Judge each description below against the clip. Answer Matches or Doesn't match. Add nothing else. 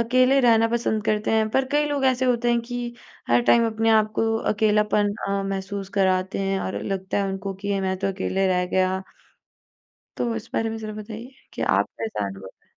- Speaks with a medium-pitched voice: Doesn't match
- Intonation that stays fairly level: Doesn't match